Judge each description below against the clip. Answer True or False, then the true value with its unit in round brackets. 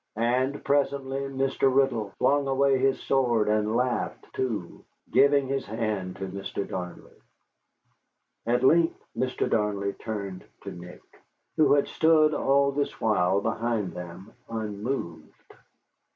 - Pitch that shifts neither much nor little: True (5.0 semitones)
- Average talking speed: False (125 wpm)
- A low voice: True (120 Hz)